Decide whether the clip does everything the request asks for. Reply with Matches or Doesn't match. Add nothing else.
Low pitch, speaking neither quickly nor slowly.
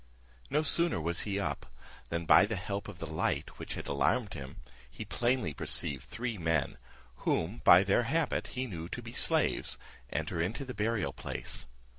Matches